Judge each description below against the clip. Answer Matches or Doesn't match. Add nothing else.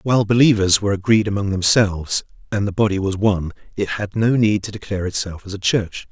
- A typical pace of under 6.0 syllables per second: Doesn't match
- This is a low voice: Matches